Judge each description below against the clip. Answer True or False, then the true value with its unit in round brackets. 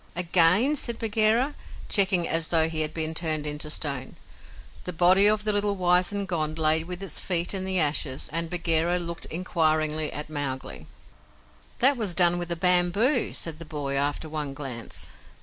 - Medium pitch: True (170 Hz)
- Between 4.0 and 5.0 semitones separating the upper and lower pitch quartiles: False (3.4 semitones)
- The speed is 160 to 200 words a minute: True (170 wpm)